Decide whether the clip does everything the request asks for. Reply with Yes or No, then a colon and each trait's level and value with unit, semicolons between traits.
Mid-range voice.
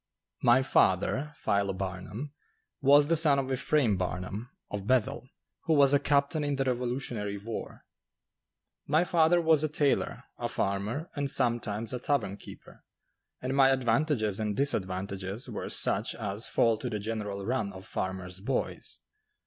No: low, 120 Hz